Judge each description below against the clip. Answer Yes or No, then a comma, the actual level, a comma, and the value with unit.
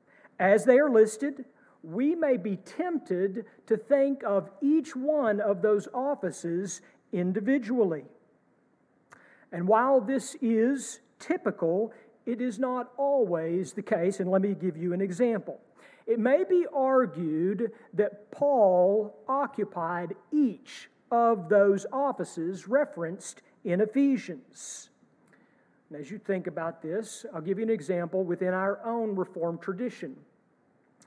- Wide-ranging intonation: Yes, wide, 5.8 semitones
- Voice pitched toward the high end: Yes, high, 215 Hz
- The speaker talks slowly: Yes, slow, 125 wpm